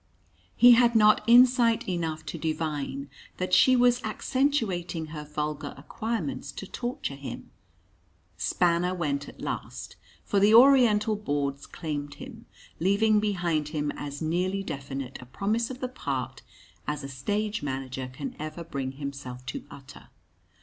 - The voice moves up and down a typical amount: No, wide, 7.5 semitones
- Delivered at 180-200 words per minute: No, average, 140 wpm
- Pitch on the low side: No, medium, 170 Hz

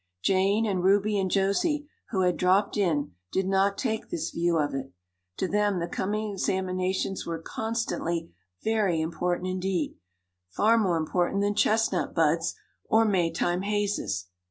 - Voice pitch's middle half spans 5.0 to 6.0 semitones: No, average, 3.0 semitones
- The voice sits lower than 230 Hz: Yes, high, 190 Hz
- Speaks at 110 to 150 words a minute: Yes, average, 145 wpm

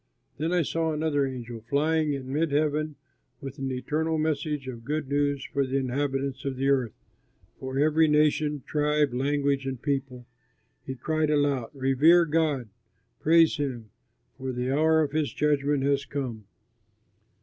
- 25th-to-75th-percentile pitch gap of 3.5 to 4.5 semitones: No, narrow, 2.5 semitones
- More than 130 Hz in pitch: Yes, medium, 140 Hz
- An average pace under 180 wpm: Yes, average, 150 wpm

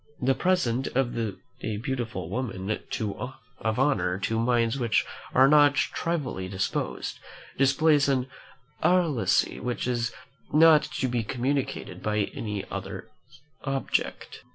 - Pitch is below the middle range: Yes, low, 125 Hz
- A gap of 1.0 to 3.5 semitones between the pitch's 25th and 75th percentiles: No, average, 3.9 semitones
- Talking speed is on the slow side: Yes, slow, 115 wpm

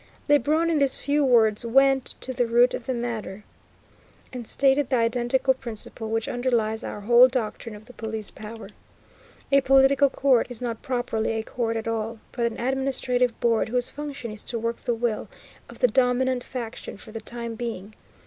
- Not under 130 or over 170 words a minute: No, average, 180 wpm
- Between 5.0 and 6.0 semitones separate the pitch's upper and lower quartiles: No, narrow, 2.6 semitones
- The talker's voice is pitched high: Yes, high, 240 Hz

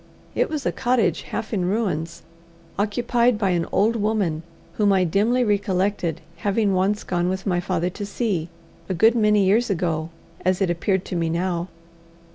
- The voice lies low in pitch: No, high, 195 Hz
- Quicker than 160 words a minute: Yes, average, 170 wpm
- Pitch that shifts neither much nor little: Yes, average, 3.3 semitones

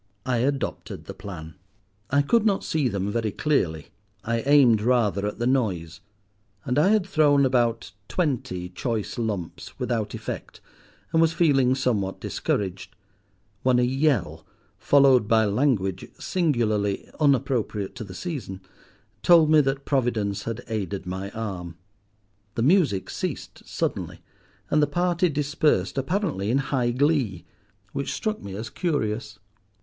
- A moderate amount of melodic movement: No, wide, 6.0 semitones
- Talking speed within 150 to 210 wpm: No, slow, 135 wpm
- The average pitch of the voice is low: Yes, low, 120 Hz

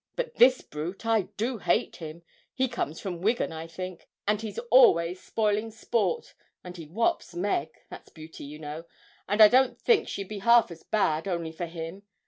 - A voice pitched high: Yes, high, 195 Hz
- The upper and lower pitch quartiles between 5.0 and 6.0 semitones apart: Yes, wide, 5.5 semitones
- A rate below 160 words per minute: No, average, 185 wpm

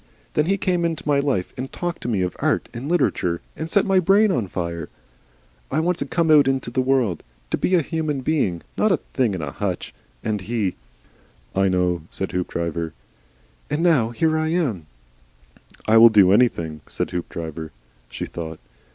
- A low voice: Yes, low, 120 Hz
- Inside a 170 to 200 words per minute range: Yes, average, 190 wpm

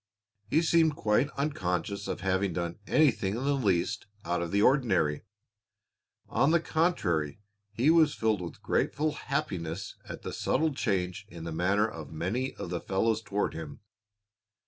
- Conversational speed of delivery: Yes, average, 155 wpm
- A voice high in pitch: No, low, 100 Hz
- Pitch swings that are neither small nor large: No, wide, 7.8 semitones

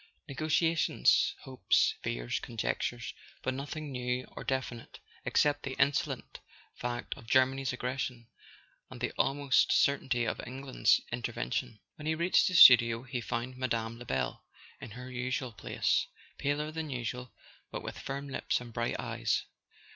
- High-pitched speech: No, low, 130 Hz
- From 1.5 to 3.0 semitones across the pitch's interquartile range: Yes, narrow, 2.5 semitones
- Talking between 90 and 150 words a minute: Yes, average, 140 wpm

